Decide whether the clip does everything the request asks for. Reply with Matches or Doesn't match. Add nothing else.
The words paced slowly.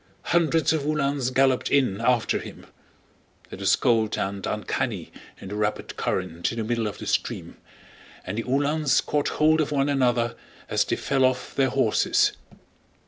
Doesn't match